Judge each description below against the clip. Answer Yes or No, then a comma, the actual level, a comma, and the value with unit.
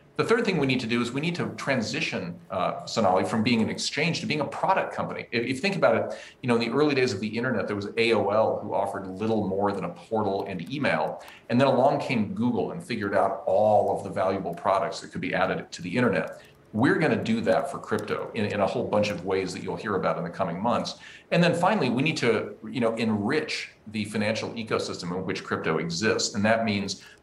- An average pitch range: Yes, average, 3.3 semitones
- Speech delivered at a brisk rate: Yes, fast, 240 wpm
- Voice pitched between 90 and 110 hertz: Yes, low, 105 Hz